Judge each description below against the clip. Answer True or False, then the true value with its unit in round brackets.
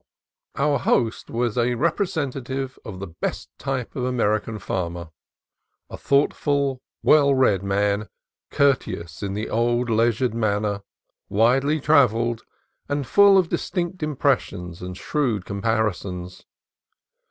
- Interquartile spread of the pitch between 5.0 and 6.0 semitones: True (5.4 semitones)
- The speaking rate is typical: False (120 wpm)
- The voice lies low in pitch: True (120 Hz)